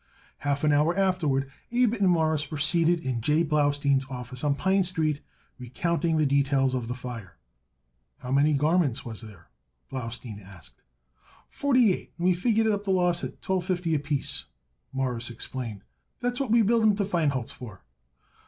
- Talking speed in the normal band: Yes, average, 170 wpm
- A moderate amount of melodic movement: No, wide, 5.8 semitones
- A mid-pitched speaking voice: Yes, medium, 150 Hz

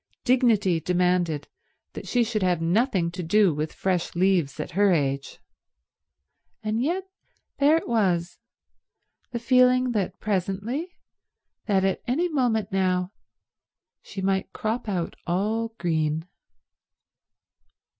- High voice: Yes, high, 195 Hz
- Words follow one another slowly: Yes, slow, 115 wpm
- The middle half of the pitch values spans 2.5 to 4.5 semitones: No, average, 4.9 semitones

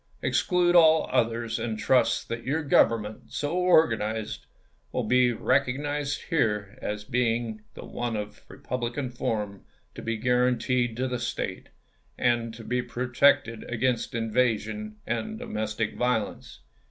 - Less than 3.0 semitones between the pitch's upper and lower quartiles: Yes, narrow, 2.5 semitones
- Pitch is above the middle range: No, low, 120 Hz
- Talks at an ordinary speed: No, slow, 130 wpm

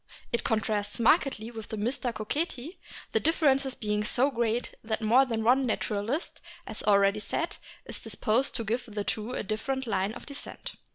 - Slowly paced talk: No, average, 175 wpm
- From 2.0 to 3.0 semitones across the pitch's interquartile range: No, average, 3.7 semitones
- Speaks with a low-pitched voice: No, high, 230 Hz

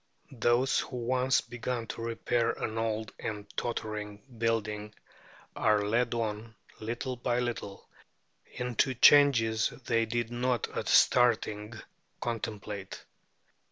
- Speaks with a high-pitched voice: No, low, 115 Hz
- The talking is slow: Yes, slow, 110 wpm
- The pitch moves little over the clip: Yes, narrow, 2.2 semitones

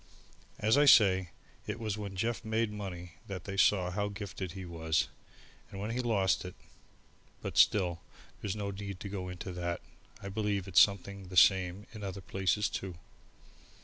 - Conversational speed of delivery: Yes, average, 175 wpm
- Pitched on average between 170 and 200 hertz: No, low, 100 Hz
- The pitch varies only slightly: Yes, narrow, 2.3 semitones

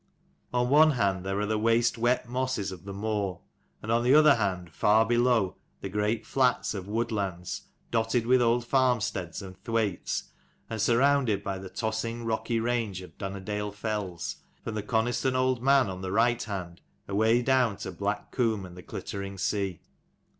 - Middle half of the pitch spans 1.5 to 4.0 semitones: Yes, average, 3.5 semitones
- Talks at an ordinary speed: Yes, average, 170 wpm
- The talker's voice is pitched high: No, low, 110 Hz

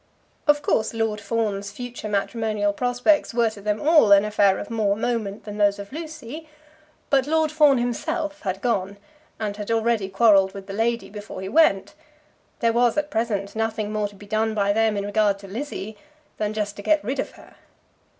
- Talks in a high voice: Yes, high, 220 Hz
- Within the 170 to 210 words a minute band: Yes, average, 190 wpm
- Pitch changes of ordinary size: Yes, average, 3.2 semitones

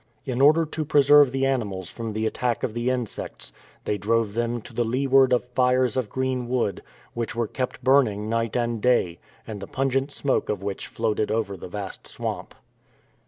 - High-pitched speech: No, low, 120 Hz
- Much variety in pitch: No, average, 3.2 semitones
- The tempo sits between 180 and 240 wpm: Yes, average, 185 wpm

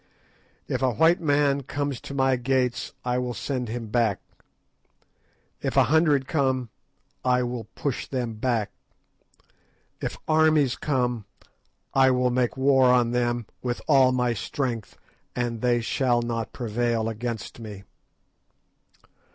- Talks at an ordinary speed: No, slow, 130 wpm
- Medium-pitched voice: No, low, 125 Hz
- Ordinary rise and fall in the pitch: No, narrow, 2.2 semitones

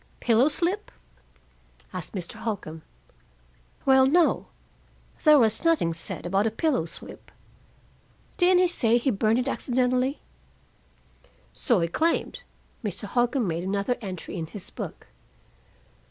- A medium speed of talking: No, slow, 125 wpm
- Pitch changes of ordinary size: No, wide, 6.0 semitones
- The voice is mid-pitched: No, high, 235 Hz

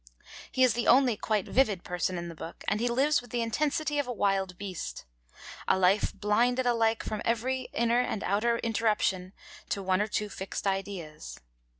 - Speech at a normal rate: Yes, average, 185 wpm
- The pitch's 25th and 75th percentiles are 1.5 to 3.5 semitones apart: No, average, 4.1 semitones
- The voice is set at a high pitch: Yes, high, 215 Hz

